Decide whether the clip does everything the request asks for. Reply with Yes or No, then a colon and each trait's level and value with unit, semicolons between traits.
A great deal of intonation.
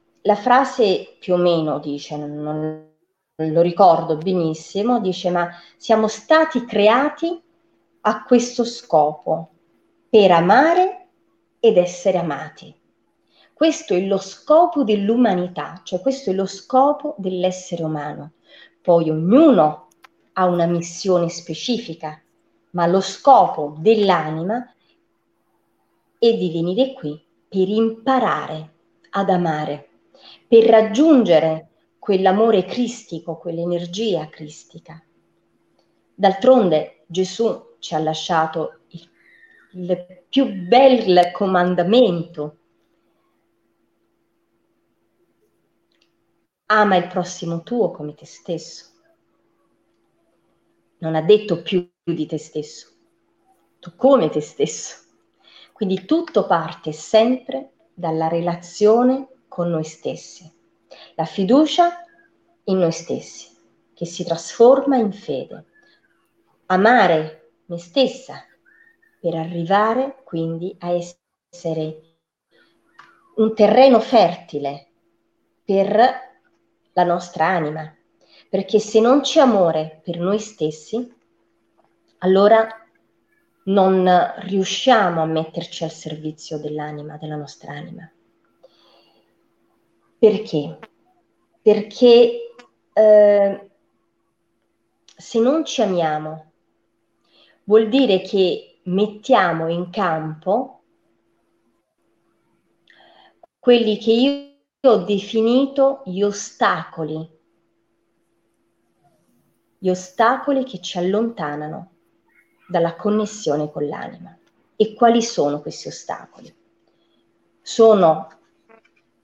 Yes: wide, 6.4 semitones